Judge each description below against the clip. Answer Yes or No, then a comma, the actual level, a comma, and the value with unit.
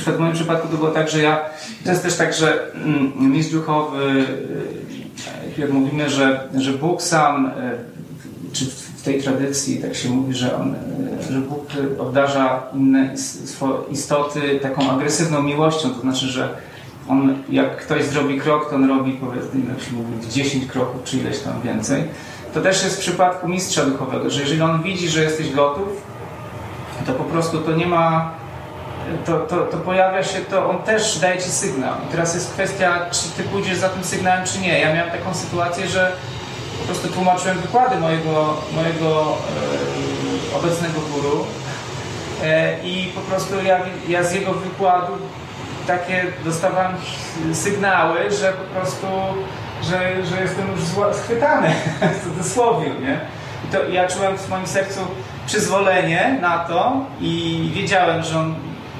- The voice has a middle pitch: Yes, medium, 160 Hz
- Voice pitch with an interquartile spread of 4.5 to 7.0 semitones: Yes, average, 5.2 semitones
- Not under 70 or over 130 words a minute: No, average, 150 wpm